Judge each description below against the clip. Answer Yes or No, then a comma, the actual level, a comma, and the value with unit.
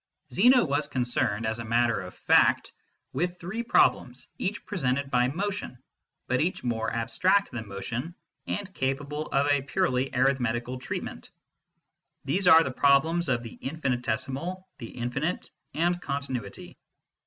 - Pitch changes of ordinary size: No, wide, 6.0 semitones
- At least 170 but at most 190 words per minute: No, average, 140 wpm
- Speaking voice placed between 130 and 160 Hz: Yes, low, 135 Hz